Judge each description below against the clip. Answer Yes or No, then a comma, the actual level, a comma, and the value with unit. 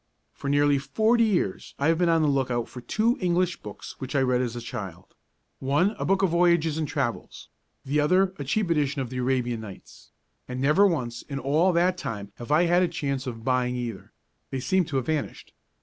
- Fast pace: Yes, fast, 215 wpm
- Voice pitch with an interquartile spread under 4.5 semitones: No, wide, 5.5 semitones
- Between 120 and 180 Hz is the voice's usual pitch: Yes, medium, 140 Hz